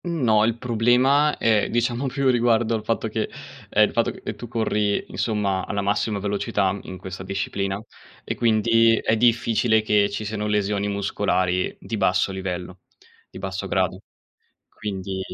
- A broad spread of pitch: No, average, 2.8 semitones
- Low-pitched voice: Yes, low, 105 Hz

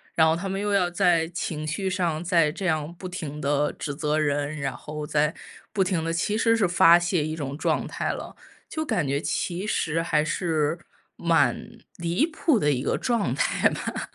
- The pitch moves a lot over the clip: No, average, 3.7 semitones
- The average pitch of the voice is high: No, medium, 165 Hz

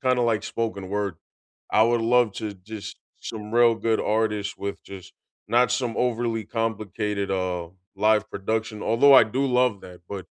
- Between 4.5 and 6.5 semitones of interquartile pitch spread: No, average, 2.8 semitones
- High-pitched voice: No, low, 110 Hz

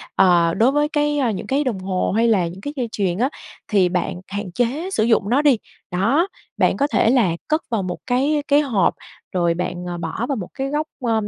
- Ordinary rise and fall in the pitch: No, wide, 7.2 semitones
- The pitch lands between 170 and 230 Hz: Yes, high, 225 Hz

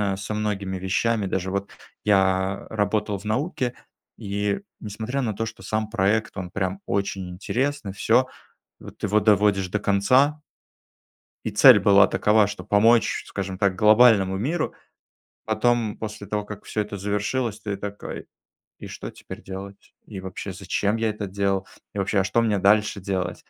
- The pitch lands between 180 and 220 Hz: No, low, 105 Hz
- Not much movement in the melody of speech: Yes, narrow, 2.0 semitones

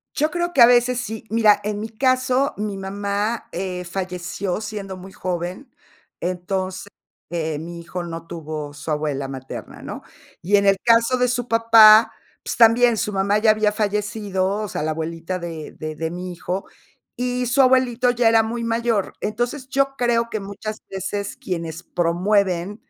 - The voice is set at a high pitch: Yes, high, 205 Hz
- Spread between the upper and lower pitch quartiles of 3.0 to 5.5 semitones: Yes, average, 4.6 semitones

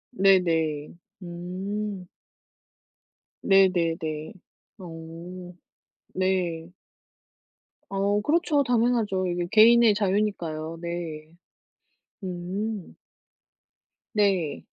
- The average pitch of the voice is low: No, medium, 185 Hz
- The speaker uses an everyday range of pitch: Yes, average, 3.6 semitones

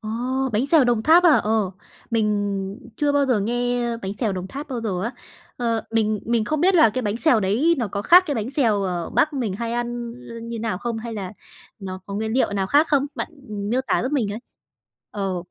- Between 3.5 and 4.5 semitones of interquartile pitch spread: Yes, average, 4.1 semitones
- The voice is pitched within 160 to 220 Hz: No, high, 230 Hz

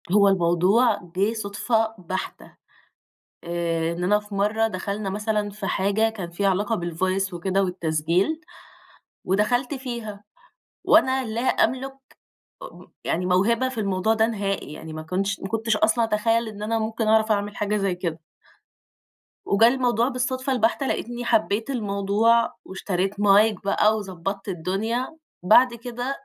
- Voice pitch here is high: Yes, high, 210 Hz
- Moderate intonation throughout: Yes, average, 3.2 semitones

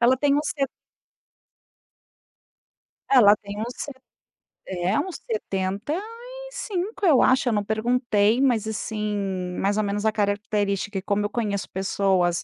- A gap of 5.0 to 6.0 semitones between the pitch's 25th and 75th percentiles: Yes, average, 5.3 semitones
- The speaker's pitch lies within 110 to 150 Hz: No, high, 215 Hz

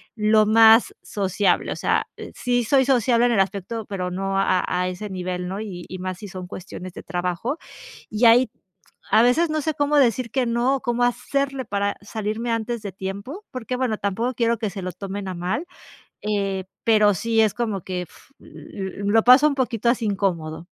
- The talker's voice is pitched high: Yes, high, 215 Hz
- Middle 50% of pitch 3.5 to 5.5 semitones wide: Yes, average, 4.1 semitones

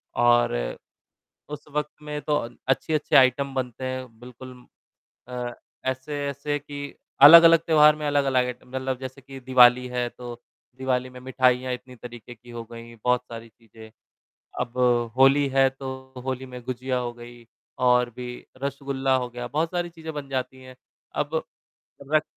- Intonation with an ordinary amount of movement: No, narrow, 2.2 semitones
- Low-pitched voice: Yes, low, 130 Hz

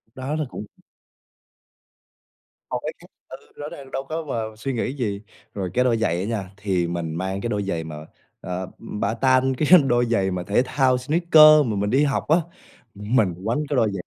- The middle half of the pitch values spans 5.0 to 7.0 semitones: Yes, wide, 5.5 semitones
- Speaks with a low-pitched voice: Yes, low, 115 Hz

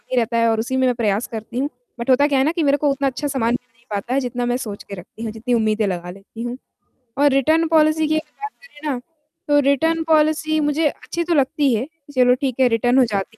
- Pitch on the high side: Yes, very high, 260 Hz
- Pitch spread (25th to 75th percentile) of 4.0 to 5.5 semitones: Yes, average, 4.5 semitones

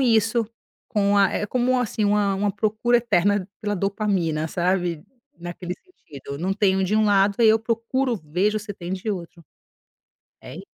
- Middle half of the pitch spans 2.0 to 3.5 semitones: Yes, average, 3.2 semitones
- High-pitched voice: Yes, high, 205 Hz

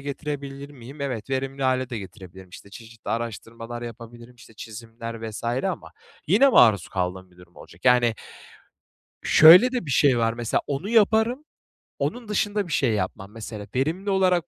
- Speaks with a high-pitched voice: No, low, 125 Hz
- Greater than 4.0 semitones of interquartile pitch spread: Yes, average, 5.2 semitones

